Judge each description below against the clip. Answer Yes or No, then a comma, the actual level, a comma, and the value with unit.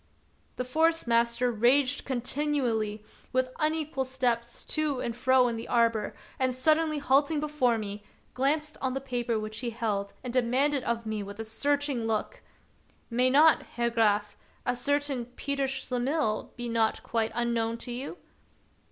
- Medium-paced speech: Yes, average, 165 wpm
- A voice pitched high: Yes, very high, 250 Hz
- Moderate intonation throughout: Yes, average, 3.4 semitones